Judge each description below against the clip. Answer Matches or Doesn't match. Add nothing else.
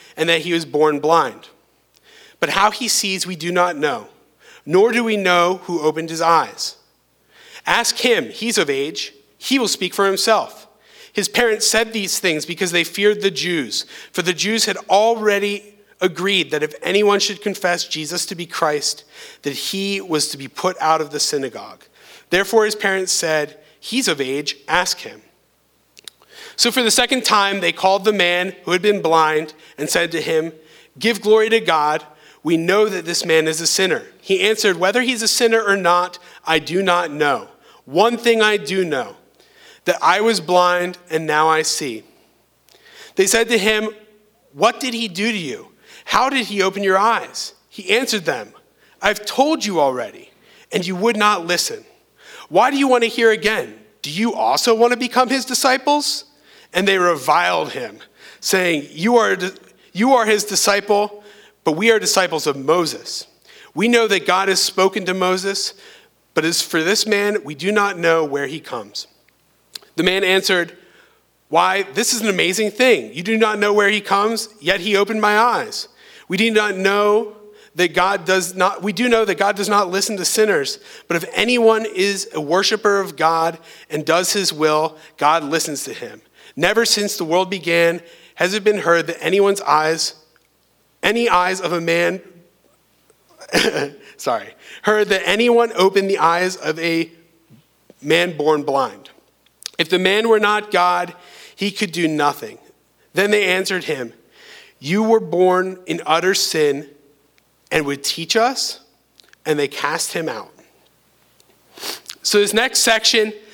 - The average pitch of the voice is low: Doesn't match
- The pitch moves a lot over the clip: Doesn't match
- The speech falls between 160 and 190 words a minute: Matches